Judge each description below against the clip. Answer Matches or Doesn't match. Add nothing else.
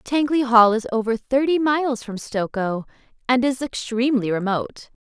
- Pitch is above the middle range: Matches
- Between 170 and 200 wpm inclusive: Doesn't match